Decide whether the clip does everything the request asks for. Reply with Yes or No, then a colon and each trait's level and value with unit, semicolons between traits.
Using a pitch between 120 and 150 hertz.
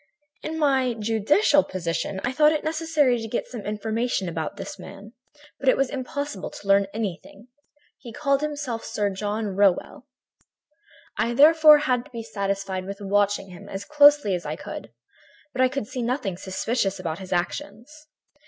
No: high, 225 Hz